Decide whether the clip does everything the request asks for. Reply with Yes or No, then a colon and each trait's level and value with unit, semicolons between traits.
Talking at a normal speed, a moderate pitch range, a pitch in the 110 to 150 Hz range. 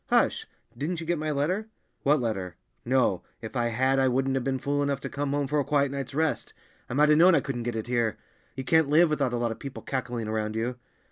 No: fast, 250 wpm; average, 3.6 semitones; low, 135 Hz